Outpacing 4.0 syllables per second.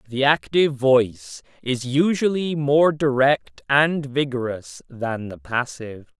No: 3.9 syllables/s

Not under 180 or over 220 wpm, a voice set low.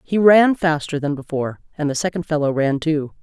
No: fast, 205 wpm; medium, 155 Hz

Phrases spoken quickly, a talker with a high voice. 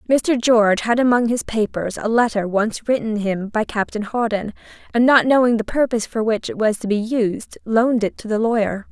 Yes: fast, 210 wpm; high, 225 Hz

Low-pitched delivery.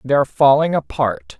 Yes: low, 130 Hz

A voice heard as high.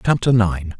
No: low, 105 Hz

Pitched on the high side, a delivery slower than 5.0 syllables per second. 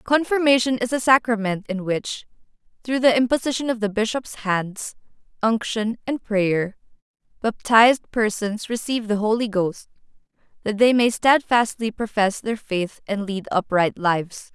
Yes: high, 220 Hz; 4.5 syllables/s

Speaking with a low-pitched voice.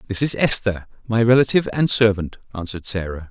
Yes: low, 110 Hz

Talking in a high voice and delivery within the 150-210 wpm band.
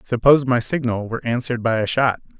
No: low, 120 Hz; average, 200 wpm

